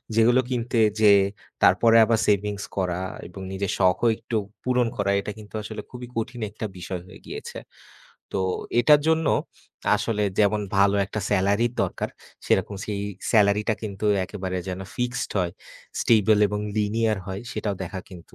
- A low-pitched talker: Yes, low, 105 Hz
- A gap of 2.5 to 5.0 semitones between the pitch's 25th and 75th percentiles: Yes, average, 2.9 semitones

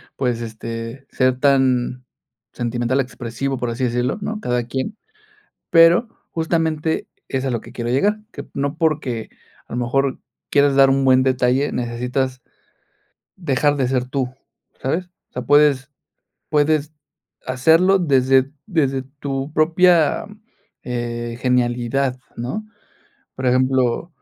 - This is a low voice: Yes, low, 130 Hz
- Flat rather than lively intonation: No, average, 3.0 semitones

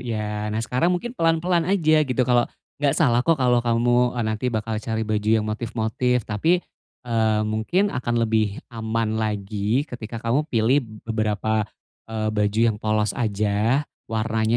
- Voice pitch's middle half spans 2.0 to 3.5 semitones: Yes, average, 2.7 semitones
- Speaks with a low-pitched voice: Yes, low, 115 Hz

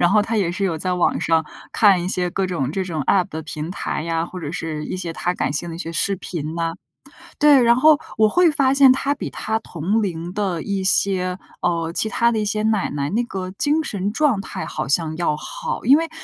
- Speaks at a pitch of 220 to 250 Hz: No, medium, 185 Hz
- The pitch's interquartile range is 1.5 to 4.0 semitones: No, average, 4.8 semitones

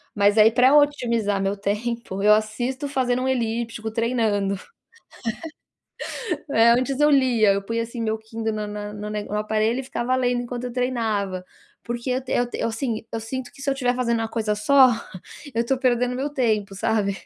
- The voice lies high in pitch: Yes, high, 230 Hz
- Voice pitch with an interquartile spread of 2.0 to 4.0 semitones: Yes, average, 2.9 semitones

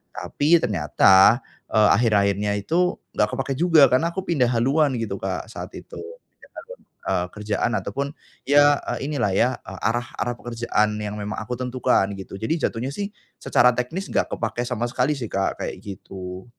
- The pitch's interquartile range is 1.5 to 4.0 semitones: No, wide, 5.5 semitones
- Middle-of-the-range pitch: No, low, 120 Hz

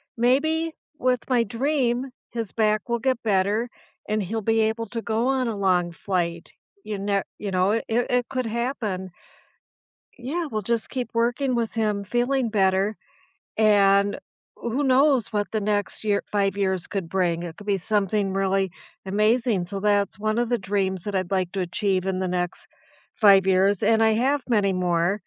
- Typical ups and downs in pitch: Yes, average, 3.5 semitones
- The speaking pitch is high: Yes, high, 210 Hz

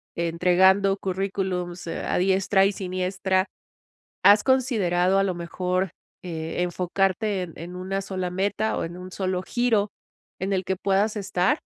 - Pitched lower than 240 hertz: Yes, high, 190 Hz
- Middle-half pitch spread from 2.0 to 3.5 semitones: No, narrow, 1.6 semitones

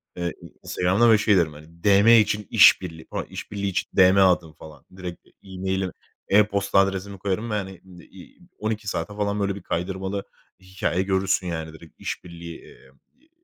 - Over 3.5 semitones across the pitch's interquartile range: No, narrow, 2.5 semitones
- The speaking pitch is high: No, very low, 95 Hz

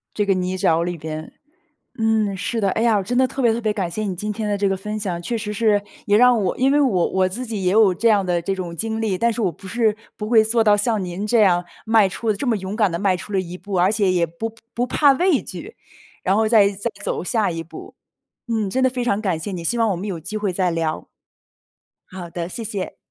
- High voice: Yes, high, 205 Hz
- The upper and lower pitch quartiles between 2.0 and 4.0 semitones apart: Yes, average, 3.5 semitones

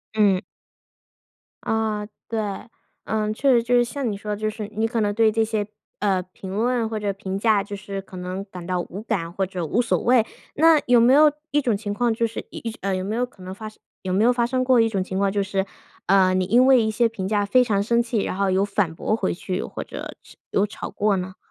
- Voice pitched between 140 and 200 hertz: No, high, 210 Hz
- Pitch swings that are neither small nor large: Yes, average, 3.2 semitones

